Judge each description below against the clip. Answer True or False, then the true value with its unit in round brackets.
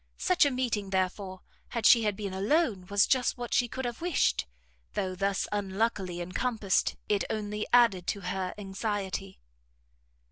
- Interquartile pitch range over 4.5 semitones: False (3.7 semitones)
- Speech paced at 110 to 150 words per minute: True (145 wpm)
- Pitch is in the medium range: False (205 Hz)